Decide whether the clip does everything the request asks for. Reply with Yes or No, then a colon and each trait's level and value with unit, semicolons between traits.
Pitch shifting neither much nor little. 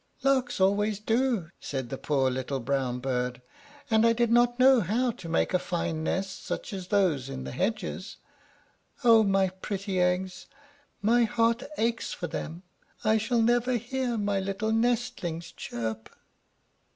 No: wide, 6.0 semitones